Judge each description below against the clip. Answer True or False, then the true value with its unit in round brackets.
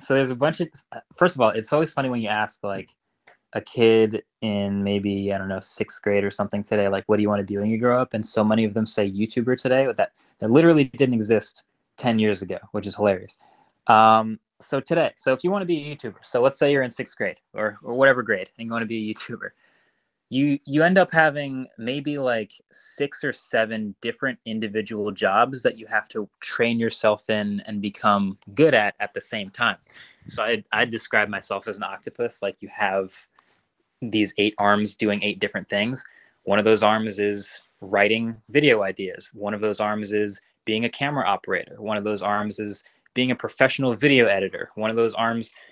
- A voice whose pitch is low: True (110 Hz)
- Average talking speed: False (215 wpm)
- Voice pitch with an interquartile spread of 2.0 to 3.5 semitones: False (3.9 semitones)